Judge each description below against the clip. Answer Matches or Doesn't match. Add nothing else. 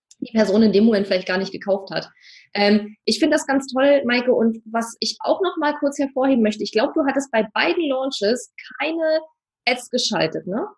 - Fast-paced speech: Matches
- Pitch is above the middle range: Matches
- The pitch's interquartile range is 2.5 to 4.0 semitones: Doesn't match